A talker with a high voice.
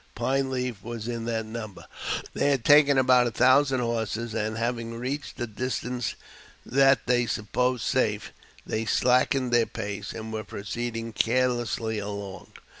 No: low, 120 Hz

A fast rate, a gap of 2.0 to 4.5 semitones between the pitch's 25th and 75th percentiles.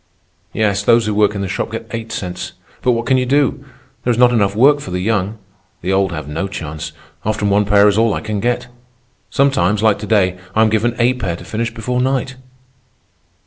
Yes: fast, 220 wpm; average, 3.4 semitones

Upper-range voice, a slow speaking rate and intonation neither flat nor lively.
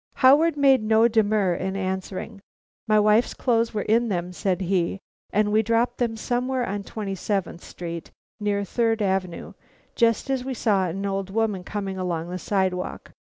No: high, 205 Hz; average, 165 wpm; average, 3.2 semitones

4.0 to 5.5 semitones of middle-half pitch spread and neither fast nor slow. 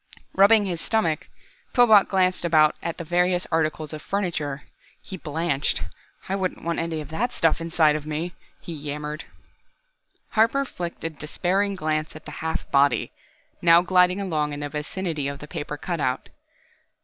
No: average, 3.4 semitones; average, 160 wpm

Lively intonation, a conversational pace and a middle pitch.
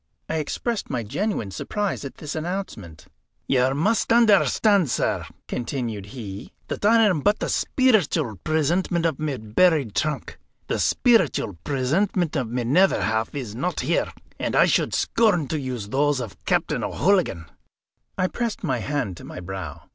Yes: wide, 8.3 semitones; average, 155 wpm; medium, 145 Hz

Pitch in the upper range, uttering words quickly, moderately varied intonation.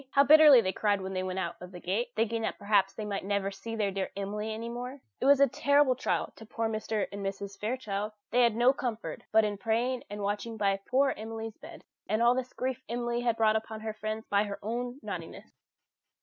Yes: high, 220 Hz; fast, 220 wpm; average, 3.1 semitones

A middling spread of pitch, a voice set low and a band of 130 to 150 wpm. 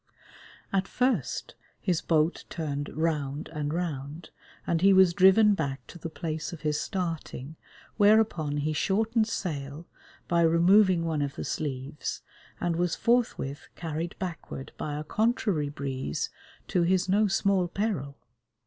No: average, 4.4 semitones; medium, 165 Hz; average, 140 wpm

